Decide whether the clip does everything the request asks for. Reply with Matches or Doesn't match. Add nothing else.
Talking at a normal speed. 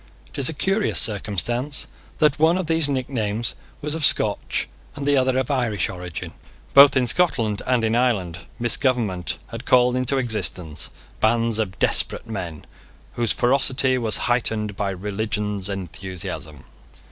Matches